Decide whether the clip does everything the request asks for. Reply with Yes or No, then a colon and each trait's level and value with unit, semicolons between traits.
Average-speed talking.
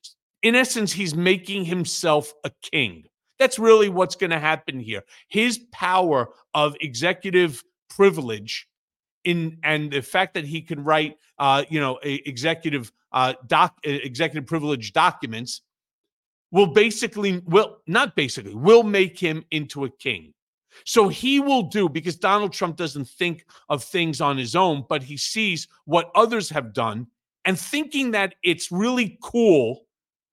Yes: average, 145 wpm